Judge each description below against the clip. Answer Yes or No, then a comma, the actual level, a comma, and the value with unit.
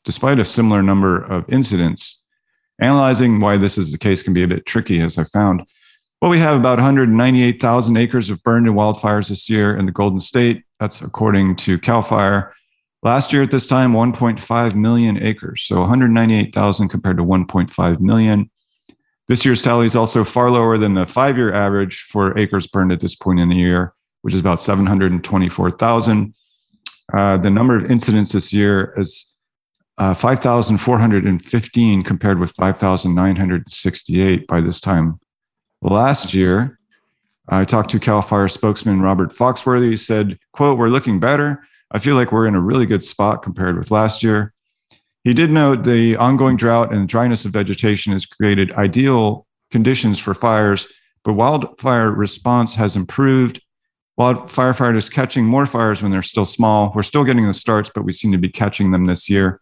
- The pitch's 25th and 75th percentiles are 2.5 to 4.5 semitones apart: Yes, average, 3.8 semitones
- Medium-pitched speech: No, low, 105 Hz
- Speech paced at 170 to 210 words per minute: Yes, average, 180 wpm